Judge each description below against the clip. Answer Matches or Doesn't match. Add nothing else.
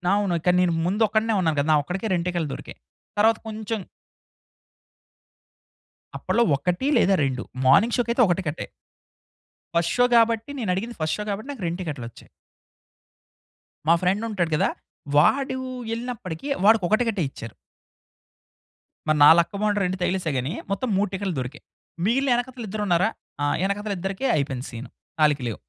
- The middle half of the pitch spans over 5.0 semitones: Matches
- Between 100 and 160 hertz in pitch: Doesn't match